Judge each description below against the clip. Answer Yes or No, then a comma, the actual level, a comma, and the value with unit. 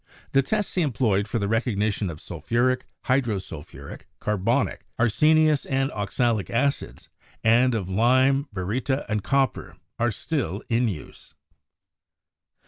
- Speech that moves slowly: Yes, slow, 125 wpm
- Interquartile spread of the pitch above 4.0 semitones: Yes, average, 4.6 semitones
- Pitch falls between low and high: No, low, 120 Hz